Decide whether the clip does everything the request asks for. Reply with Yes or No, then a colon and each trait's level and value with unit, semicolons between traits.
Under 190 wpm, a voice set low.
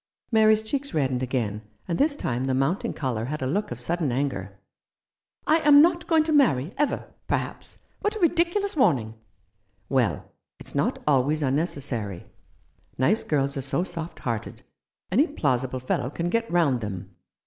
No: average, 170 wpm; medium, 150 Hz